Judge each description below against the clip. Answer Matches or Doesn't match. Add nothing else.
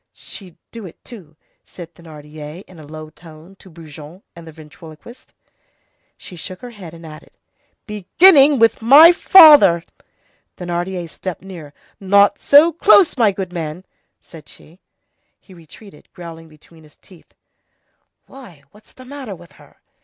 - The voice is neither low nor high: Matches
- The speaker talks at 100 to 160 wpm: Matches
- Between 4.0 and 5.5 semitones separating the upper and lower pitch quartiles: Matches